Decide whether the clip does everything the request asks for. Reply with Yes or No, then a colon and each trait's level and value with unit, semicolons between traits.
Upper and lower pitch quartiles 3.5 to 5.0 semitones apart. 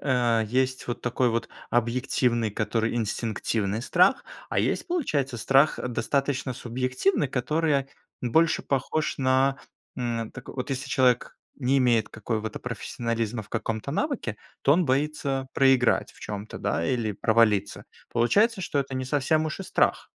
No: average, 3.1 semitones